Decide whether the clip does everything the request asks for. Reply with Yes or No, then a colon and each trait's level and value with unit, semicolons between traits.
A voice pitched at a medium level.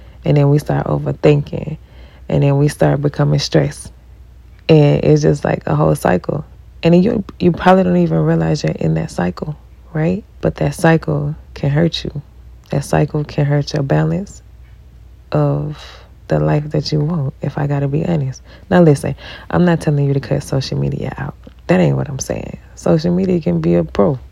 Yes: medium, 145 Hz